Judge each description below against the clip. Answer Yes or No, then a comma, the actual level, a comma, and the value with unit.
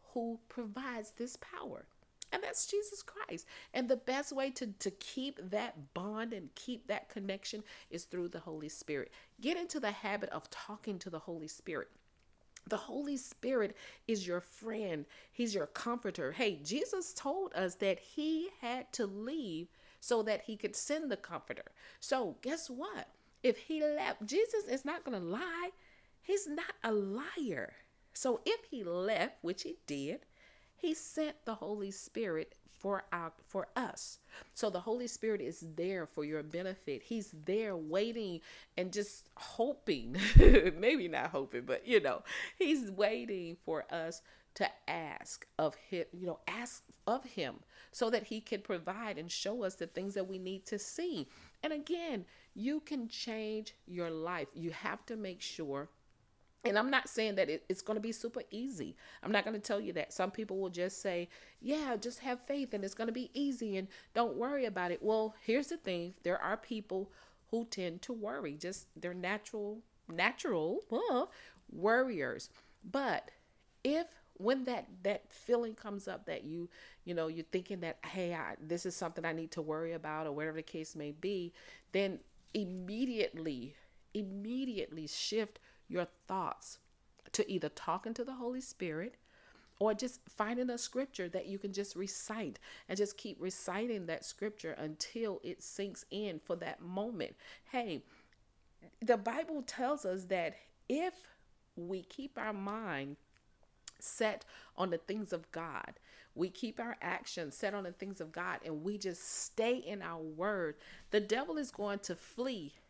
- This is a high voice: Yes, high, 210 Hz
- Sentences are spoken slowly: No, average, 170 wpm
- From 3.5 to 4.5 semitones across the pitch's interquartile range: No, wide, 5.6 semitones